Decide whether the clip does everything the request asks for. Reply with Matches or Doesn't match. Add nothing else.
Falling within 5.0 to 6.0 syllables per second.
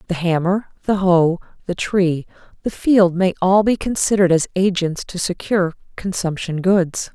Doesn't match